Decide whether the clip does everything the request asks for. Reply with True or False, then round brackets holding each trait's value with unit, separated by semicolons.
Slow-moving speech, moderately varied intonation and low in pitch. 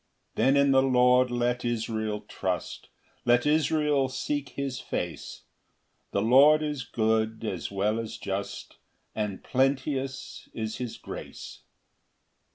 True (130 wpm; 3.7 semitones; 125 Hz)